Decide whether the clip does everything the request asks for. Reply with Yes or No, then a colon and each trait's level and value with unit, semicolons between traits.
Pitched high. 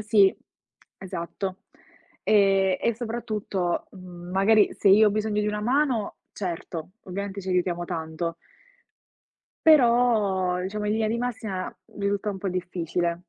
Yes: high, 195 Hz